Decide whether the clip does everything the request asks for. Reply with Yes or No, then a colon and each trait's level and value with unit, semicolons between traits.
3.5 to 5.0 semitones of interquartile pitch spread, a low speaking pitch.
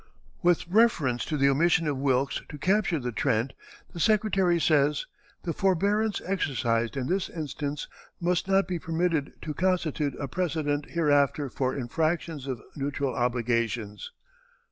No: average, 4.6 semitones; medium, 150 Hz